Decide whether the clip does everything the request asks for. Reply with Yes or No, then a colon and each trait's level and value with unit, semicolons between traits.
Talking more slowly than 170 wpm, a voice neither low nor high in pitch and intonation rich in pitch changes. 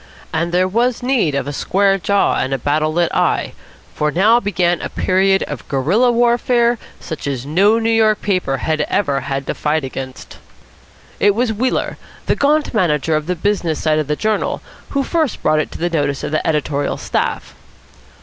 No: average, 190 wpm; medium, 175 Hz; wide, 6.5 semitones